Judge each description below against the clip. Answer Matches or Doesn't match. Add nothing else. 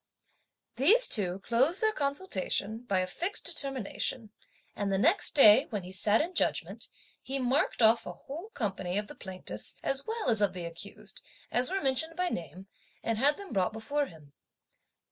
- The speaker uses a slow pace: Doesn't match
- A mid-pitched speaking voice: Doesn't match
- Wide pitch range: Matches